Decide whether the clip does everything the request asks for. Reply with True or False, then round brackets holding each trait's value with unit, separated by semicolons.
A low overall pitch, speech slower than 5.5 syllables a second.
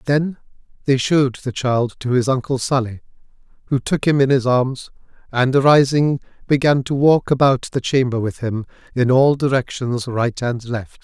True (130 Hz; 4.7 syllables/s)